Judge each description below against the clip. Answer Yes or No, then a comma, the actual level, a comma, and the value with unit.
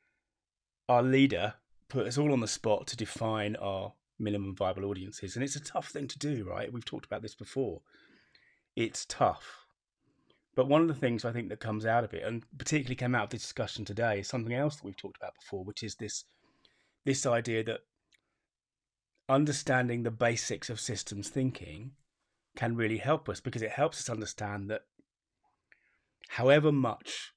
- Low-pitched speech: Yes, low, 120 Hz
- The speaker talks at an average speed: Yes, average, 180 wpm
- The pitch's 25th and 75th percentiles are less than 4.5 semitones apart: Yes, average, 4.1 semitones